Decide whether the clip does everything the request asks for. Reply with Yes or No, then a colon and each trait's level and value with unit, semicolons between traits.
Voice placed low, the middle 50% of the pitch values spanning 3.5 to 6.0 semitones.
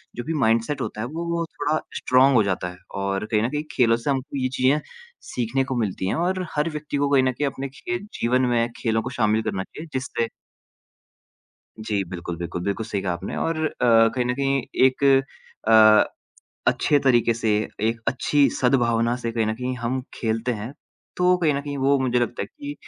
Yes: low, 125 Hz; average, 3.9 semitones